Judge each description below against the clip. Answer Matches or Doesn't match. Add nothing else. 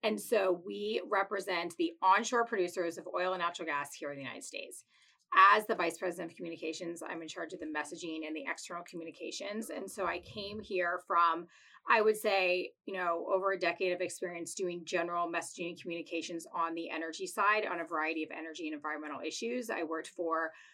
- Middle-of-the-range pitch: Matches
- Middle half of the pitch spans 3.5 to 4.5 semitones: Doesn't match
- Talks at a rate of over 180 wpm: Matches